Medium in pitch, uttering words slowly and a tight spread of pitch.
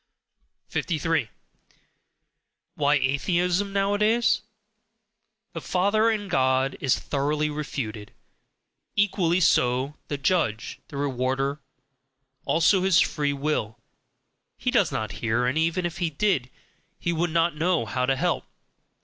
No: medium, 150 Hz; slow, 115 wpm; average, 5.3 semitones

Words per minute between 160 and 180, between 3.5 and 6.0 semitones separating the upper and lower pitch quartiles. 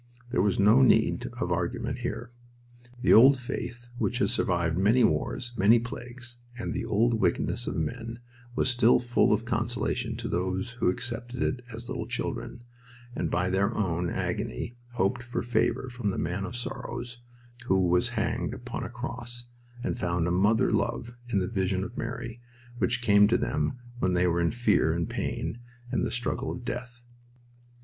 Yes: average, 175 wpm; average, 3.9 semitones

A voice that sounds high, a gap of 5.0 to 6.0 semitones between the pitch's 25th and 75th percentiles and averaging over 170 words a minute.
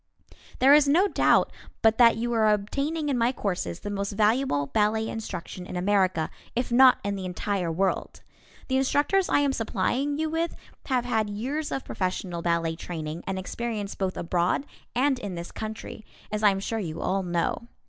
Yes: high, 215 Hz; wide, 5.6 semitones; average, 180 wpm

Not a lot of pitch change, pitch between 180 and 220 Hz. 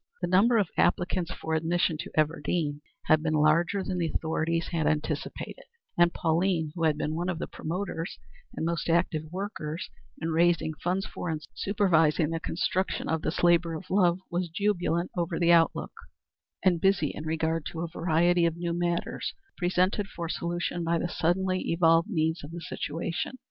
No: narrow, 1.8 semitones; medium, 170 Hz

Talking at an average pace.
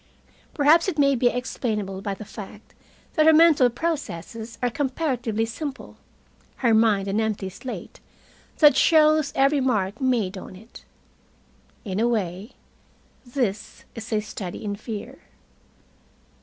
No: slow, 130 wpm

